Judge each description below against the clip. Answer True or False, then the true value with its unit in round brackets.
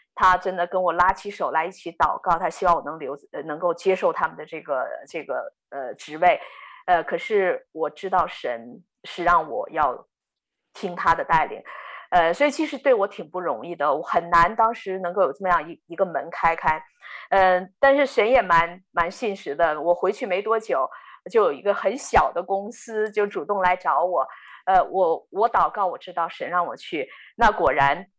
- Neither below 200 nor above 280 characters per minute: True (270 characters per minute)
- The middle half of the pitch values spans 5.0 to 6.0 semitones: False (4.6 semitones)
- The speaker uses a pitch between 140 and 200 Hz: True (185 Hz)